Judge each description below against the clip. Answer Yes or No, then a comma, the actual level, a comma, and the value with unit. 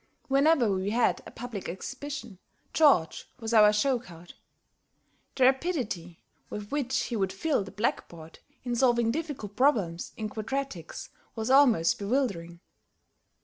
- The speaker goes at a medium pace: No, slow, 130 wpm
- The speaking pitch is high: Yes, high, 230 Hz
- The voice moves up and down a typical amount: No, wide, 5.7 semitones